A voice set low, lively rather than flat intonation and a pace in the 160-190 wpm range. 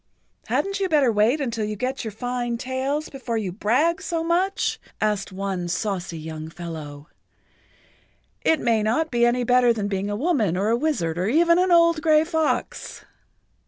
No: high, 240 Hz; wide, 7.6 semitones; average, 175 wpm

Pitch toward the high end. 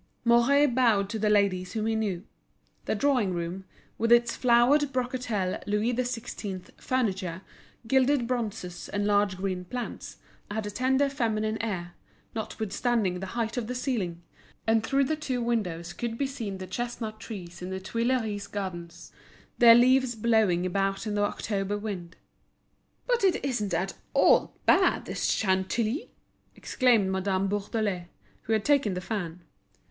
Yes: high, 215 Hz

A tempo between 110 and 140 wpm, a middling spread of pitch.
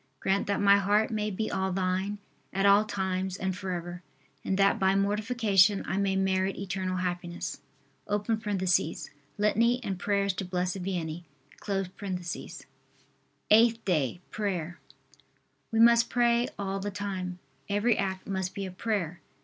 No: slow, 135 wpm; narrow, 2.0 semitones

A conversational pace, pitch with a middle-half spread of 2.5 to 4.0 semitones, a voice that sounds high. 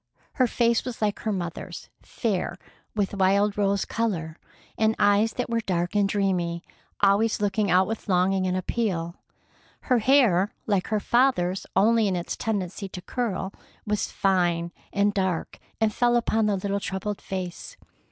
Yes: average, 155 wpm; average, 3.0 semitones; high, 200 Hz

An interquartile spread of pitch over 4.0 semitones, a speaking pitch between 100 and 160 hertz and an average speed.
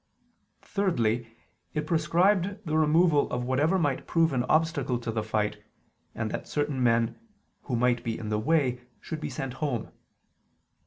Yes: average, 5.2 semitones; low, 135 Hz; average, 155 wpm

